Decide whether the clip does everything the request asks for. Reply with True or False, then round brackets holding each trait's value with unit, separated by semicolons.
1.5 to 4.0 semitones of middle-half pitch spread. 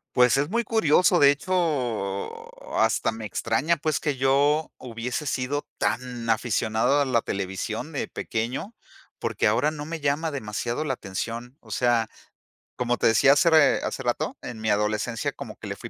False (4.7 semitones)